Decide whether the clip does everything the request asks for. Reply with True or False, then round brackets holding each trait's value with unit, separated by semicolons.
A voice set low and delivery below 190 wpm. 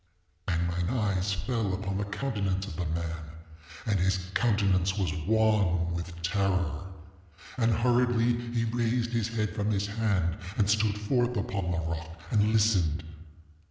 True (100 Hz; 150 wpm)